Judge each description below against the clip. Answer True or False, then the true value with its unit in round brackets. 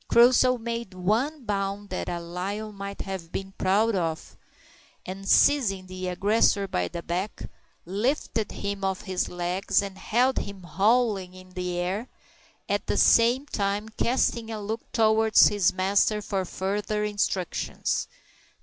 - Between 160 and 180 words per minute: False (140 wpm)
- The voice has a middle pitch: False (200 Hz)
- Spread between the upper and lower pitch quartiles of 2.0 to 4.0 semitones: True (3.0 semitones)